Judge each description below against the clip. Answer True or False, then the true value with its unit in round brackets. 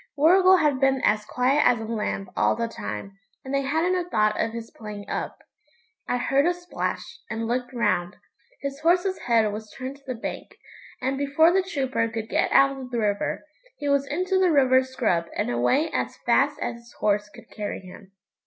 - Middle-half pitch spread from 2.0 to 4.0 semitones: False (4.9 semitones)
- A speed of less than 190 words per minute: False (200 wpm)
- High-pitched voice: True (255 Hz)